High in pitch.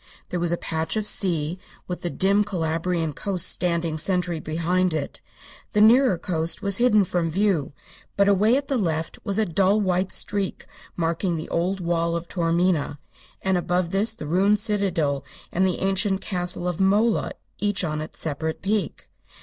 No: medium, 180 Hz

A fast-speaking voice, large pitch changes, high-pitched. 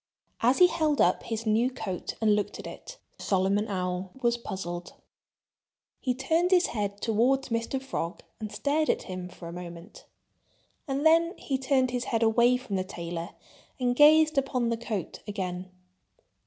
No: average, 165 wpm; wide, 6.0 semitones; high, 230 Hz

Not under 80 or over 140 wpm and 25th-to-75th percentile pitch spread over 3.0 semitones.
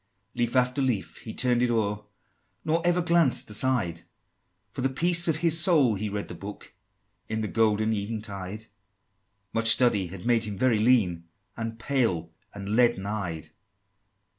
No: average, 160 wpm; average, 3.9 semitones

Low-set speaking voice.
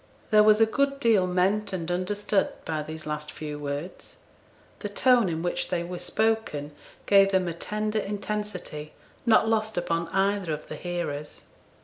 No: medium, 185 Hz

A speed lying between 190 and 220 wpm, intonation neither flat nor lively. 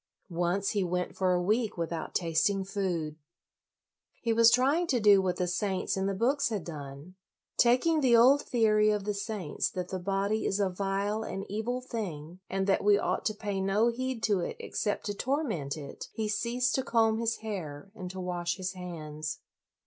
Yes: average, 195 wpm; average, 3.8 semitones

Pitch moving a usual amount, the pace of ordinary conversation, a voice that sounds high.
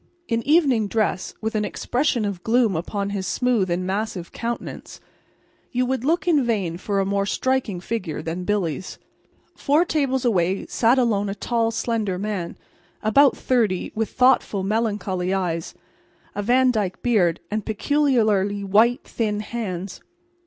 Yes: average, 4.1 semitones; average, 145 wpm; high, 215 Hz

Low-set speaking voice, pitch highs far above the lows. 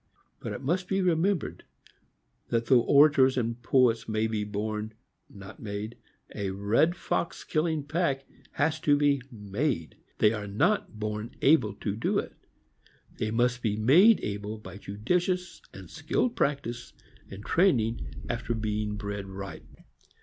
Yes: low, 115 Hz; wide, 6.0 semitones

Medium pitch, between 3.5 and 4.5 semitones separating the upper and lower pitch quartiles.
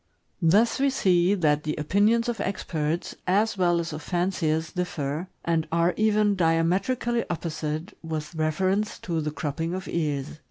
Yes: medium, 170 Hz; average, 3.9 semitones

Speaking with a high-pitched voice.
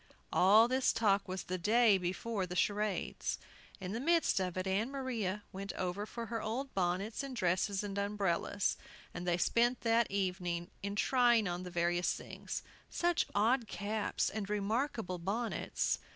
Yes: high, 205 Hz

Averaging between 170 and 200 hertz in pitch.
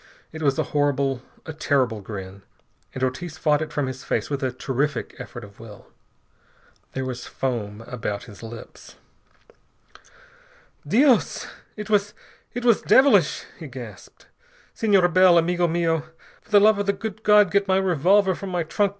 No: medium, 160 Hz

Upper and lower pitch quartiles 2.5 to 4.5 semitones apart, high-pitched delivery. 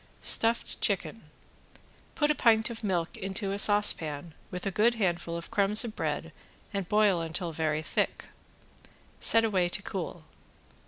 Yes: average, 4.1 semitones; high, 195 Hz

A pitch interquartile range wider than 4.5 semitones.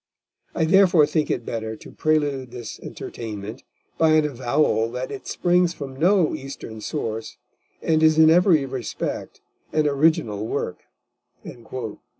Yes: average, 5.0 semitones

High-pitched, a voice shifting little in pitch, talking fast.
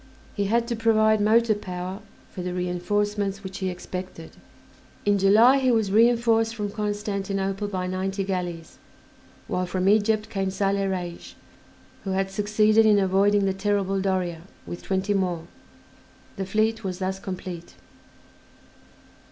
No: high, 195 Hz; narrow, 2.2 semitones; slow, 135 wpm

